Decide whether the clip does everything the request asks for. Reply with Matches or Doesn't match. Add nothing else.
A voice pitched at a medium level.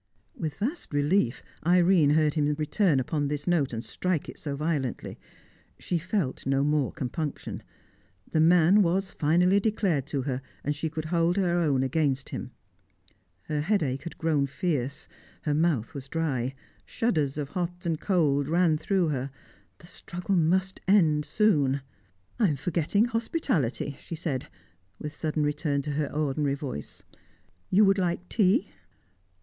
Matches